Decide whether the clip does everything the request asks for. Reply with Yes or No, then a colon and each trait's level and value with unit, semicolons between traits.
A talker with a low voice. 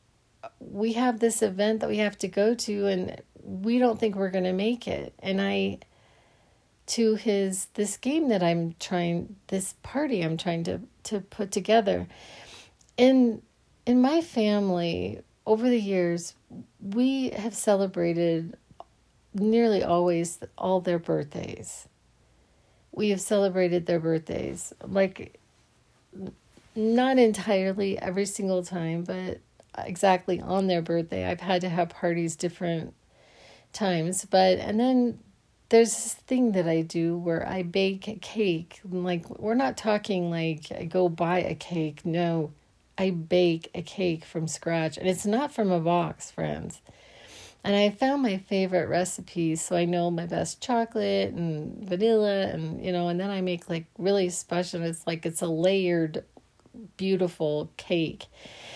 No: medium, 185 Hz